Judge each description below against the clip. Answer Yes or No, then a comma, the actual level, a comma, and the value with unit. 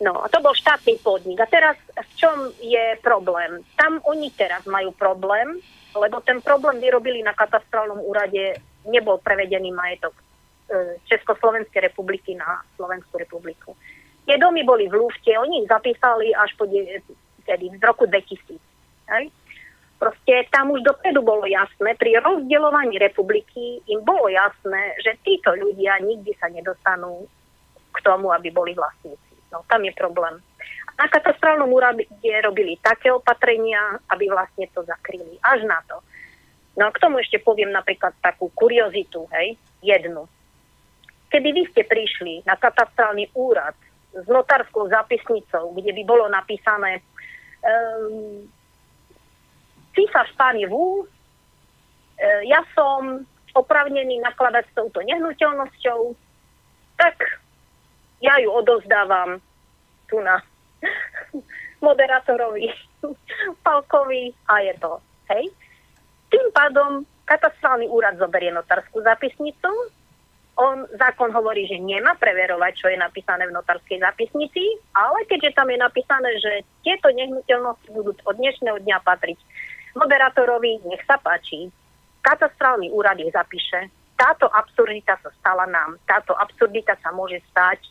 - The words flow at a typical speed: Yes, average, 125 wpm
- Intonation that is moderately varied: No, wide, 6.7 semitones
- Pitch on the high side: Yes, high, 225 Hz